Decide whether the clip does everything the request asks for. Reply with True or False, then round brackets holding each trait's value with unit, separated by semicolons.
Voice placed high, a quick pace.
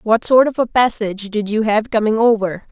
True (220 Hz; 220 wpm)